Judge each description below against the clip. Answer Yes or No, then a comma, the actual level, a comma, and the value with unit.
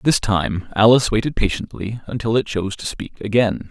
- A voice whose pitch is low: Yes, low, 110 Hz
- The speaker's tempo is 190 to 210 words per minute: No, average, 180 wpm